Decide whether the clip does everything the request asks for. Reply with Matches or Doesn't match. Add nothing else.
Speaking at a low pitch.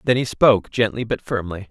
Matches